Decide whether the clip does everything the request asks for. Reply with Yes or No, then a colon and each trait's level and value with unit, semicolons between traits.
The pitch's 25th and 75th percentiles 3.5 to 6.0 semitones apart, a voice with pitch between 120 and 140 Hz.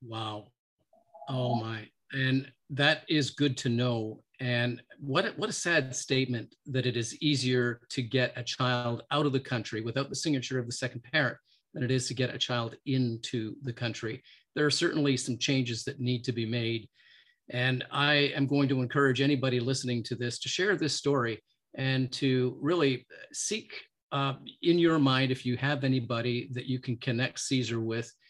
No: narrow, 2.5 semitones; low, 130 Hz